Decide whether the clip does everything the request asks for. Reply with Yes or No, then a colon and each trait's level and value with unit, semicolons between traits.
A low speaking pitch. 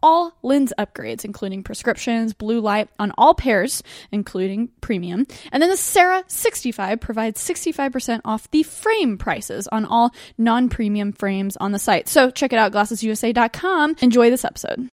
No: high, 235 Hz